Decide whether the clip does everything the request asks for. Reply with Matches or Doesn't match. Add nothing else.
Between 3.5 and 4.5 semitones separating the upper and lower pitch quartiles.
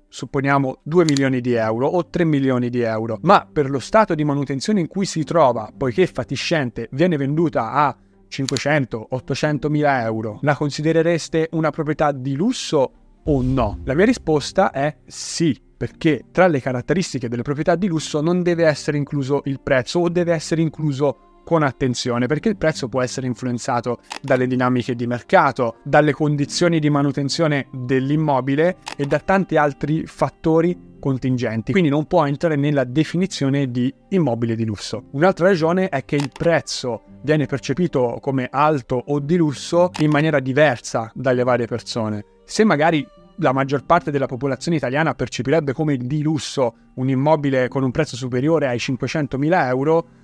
Matches